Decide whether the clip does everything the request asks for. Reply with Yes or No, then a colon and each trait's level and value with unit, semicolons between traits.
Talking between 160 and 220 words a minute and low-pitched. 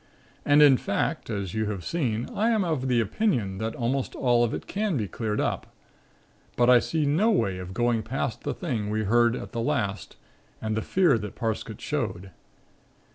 Yes: average, 190 wpm; low, 120 Hz